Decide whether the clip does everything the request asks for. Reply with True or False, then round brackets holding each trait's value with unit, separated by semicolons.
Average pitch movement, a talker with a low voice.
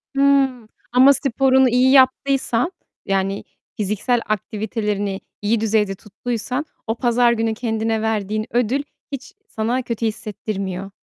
False (3.2 semitones; 225 Hz)